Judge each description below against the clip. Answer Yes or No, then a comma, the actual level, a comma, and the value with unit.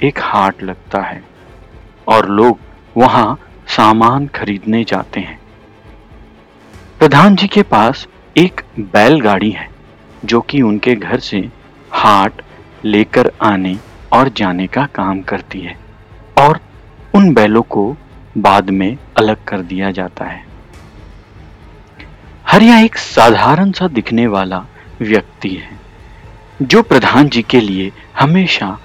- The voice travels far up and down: No, average, 4.4 semitones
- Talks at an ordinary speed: No, slow, 90 wpm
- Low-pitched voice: Yes, low, 110 Hz